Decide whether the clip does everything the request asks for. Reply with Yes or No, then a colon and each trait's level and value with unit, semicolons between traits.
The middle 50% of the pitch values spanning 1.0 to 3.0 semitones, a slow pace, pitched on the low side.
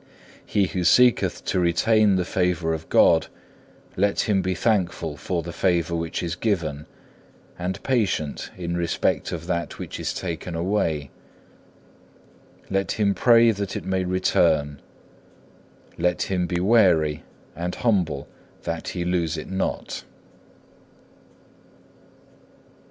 Yes: average, 2.7 semitones; slow, 125 wpm; very low, 90 Hz